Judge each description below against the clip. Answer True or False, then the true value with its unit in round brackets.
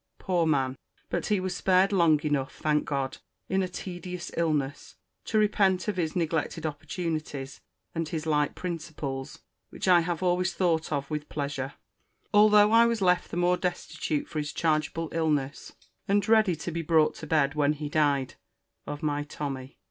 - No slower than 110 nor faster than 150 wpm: False (165 wpm)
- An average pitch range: True (3.6 semitones)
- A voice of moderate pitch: True (160 Hz)